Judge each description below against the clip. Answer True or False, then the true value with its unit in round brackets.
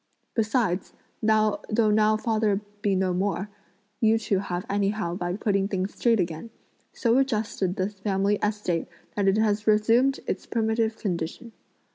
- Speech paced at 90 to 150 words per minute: True (140 wpm)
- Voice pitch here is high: True (210 Hz)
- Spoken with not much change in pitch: True (2.3 semitones)